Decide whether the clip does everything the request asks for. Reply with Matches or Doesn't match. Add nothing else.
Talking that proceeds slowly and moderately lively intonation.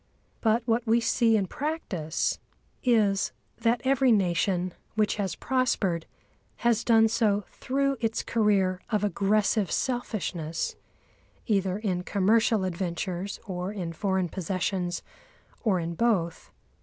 Matches